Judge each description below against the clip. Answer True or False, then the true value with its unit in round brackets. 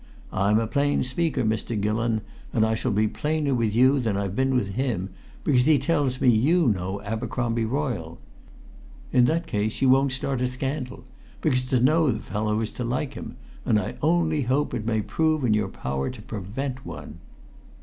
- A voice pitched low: True (125 Hz)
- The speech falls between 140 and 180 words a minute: False (190 wpm)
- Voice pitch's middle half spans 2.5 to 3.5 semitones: False (4.3 semitones)